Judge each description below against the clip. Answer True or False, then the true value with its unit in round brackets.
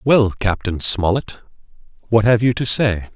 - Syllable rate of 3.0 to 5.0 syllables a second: True (4.4 syllables/s)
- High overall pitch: False (110 Hz)